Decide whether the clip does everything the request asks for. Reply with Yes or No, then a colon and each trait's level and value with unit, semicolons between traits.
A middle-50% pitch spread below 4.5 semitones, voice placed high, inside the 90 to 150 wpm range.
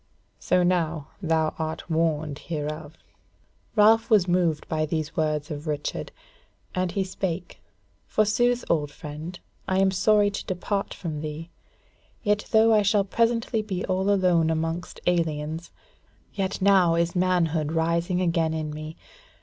No: average, 3.4 semitones; medium, 170 Hz; average, 140 wpm